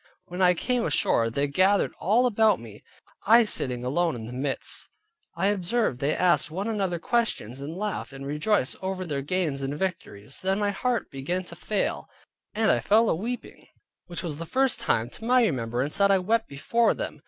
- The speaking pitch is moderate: Yes, medium, 180 Hz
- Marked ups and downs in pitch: Yes, wide, 7.3 semitones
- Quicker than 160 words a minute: Yes, average, 190 wpm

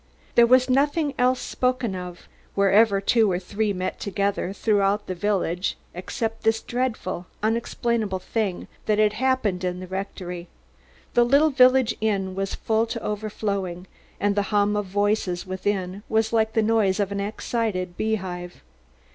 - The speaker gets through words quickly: No, average, 150 wpm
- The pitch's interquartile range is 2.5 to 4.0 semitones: Yes, average, 3.2 semitones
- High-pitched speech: Yes, high, 205 Hz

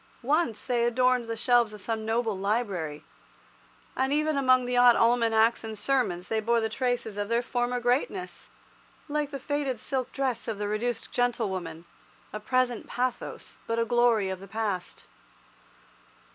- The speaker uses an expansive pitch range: No, average, 2.7 semitones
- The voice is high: Yes, high, 235 Hz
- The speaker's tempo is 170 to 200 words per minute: No, average, 160 wpm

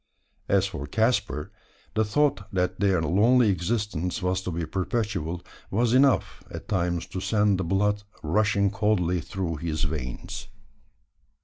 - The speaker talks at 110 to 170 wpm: Yes, slow, 135 wpm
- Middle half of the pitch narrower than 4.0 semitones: Yes, average, 3.6 semitones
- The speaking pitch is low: Yes, very low, 95 Hz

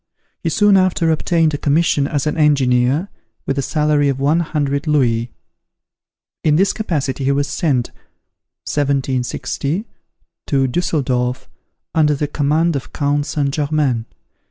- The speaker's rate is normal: No, slow, 130 wpm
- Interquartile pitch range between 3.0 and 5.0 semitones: No, narrow, 2.4 semitones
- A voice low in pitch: No, medium, 145 Hz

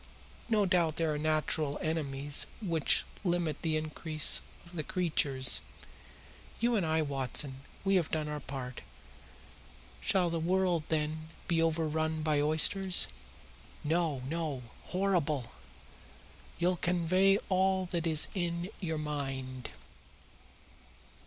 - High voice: No, medium, 160 Hz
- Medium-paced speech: No, slow, 115 wpm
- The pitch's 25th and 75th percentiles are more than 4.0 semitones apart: No, average, 2.9 semitones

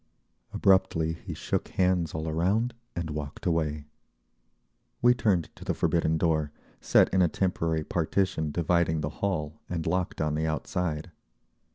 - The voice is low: Yes, very low, 80 Hz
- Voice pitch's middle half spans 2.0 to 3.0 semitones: Yes, narrow, 2.6 semitones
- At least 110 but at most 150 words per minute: Yes, average, 145 wpm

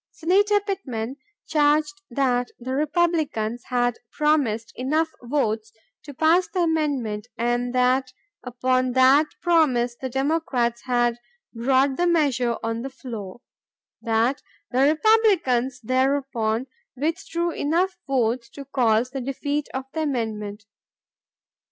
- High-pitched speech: Yes, very high, 260 Hz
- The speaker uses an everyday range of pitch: Yes, average, 4.2 semitones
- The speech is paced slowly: Yes, slow, 115 wpm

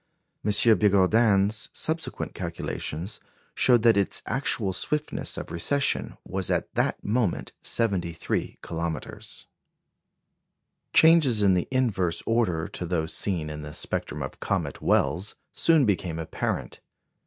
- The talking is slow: Yes, slow, 120 wpm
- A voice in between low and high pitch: No, low, 100 Hz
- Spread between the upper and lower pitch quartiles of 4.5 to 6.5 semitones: Yes, wide, 5.5 semitones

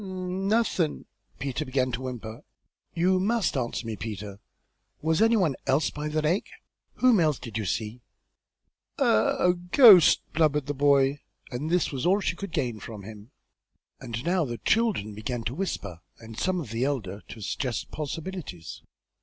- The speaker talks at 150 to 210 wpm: Yes, average, 170 wpm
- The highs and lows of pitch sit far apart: Yes, wide, 7.7 semitones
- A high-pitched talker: No, medium, 140 Hz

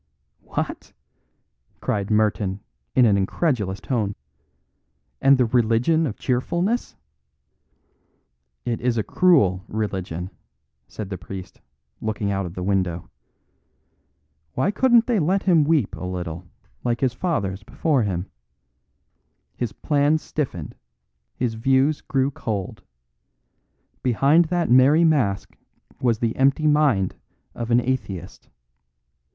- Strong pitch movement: Yes, wide, 6.9 semitones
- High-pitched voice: No, low, 120 Hz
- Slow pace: Yes, slow, 115 wpm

